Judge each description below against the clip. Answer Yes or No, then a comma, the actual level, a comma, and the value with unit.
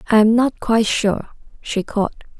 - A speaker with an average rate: Yes, average, 175 wpm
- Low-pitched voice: No, high, 220 Hz